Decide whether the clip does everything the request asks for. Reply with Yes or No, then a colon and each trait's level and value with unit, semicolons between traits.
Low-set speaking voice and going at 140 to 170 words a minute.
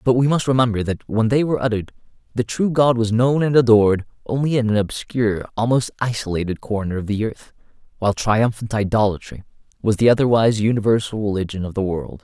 No: low, 115 Hz; average, 180 wpm